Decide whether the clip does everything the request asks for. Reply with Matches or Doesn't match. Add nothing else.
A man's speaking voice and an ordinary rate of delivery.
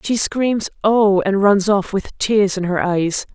Doesn't match